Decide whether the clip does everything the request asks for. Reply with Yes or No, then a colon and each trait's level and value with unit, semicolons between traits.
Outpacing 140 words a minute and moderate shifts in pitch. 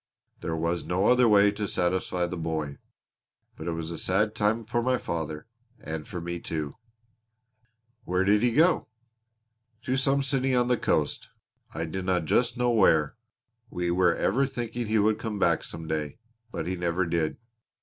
No: average, 170 wpm; wide, 5.8 semitones